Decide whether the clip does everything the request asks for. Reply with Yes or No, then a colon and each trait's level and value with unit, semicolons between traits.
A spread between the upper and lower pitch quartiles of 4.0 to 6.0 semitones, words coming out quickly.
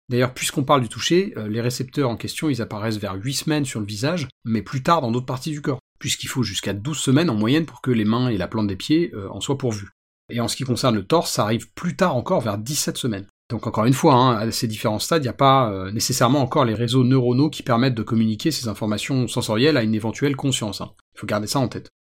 Yes: average, 4.7 semitones; fast, 265 wpm